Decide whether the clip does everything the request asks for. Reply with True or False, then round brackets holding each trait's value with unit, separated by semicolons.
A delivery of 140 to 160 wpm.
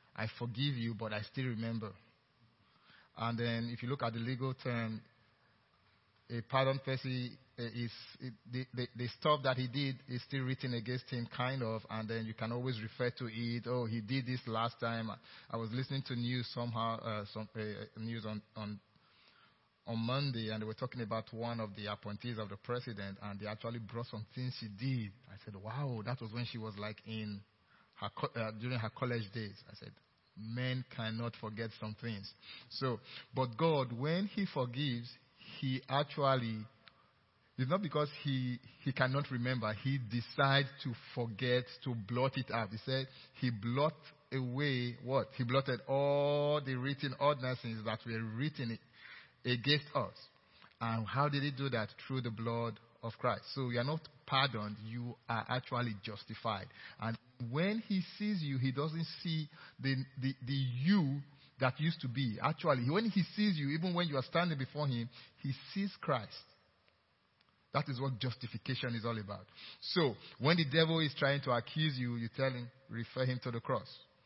False (180 wpm)